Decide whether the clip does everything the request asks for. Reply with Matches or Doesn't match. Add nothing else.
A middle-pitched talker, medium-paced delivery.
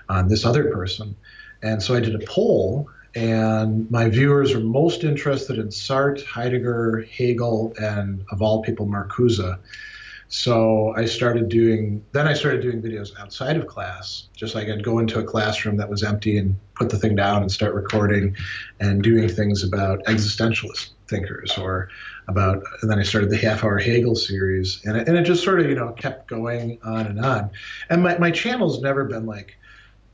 Doesn't match